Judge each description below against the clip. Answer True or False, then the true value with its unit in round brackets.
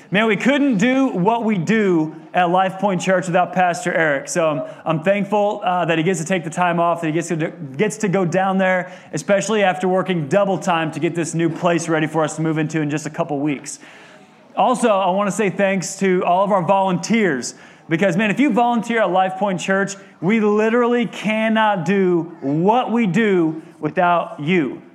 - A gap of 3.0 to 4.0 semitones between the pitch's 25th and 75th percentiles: True (3.6 semitones)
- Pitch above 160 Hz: True (185 Hz)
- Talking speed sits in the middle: False (210 wpm)